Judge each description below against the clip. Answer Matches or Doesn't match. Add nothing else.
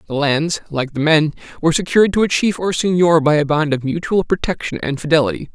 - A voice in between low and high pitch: Matches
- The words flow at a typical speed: Doesn't match